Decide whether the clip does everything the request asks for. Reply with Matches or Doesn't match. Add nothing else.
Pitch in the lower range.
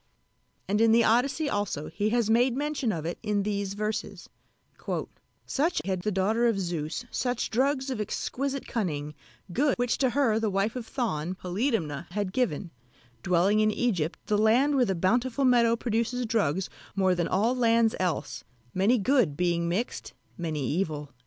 Doesn't match